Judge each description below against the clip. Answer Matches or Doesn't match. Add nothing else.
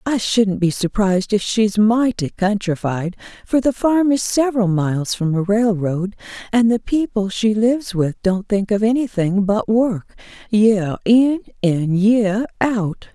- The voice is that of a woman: Matches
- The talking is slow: Doesn't match